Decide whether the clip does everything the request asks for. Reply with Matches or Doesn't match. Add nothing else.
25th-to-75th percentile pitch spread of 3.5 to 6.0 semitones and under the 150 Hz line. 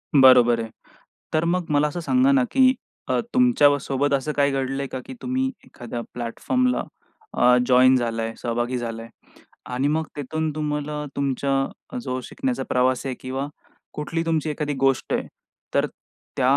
Matches